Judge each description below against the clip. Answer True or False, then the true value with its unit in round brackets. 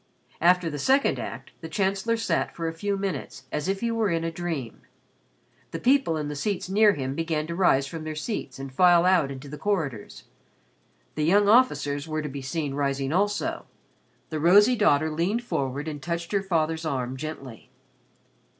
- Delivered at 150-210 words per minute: True (185 wpm)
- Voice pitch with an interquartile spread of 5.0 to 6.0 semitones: True (5.3 semitones)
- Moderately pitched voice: True (165 Hz)